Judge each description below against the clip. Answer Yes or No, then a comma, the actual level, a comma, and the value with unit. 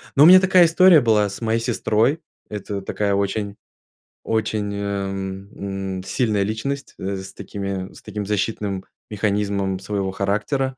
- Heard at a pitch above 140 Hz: No, low, 105 Hz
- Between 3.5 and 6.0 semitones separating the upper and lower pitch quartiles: No, narrow, 2.4 semitones